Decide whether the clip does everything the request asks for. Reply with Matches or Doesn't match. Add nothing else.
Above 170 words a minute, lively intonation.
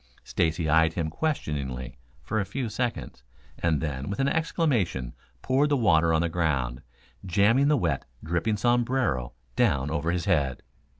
Doesn't match